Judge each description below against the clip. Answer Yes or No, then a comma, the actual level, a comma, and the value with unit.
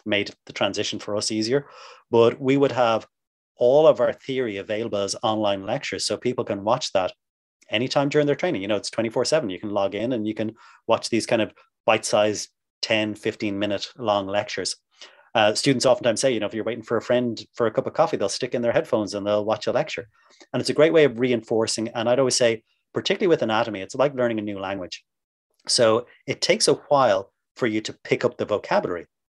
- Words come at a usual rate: No, fast, 225 wpm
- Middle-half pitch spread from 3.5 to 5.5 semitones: No, average, 3.0 semitones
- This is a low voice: Yes, low, 110 Hz